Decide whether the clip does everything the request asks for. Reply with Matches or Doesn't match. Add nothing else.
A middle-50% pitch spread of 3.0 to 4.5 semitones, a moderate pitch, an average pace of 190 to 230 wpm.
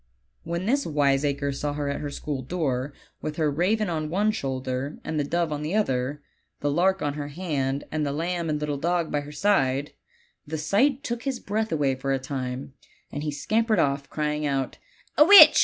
Matches